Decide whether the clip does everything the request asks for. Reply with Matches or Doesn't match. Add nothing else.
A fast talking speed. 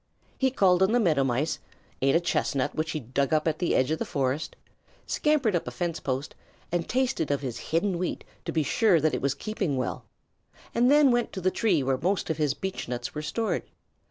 Matches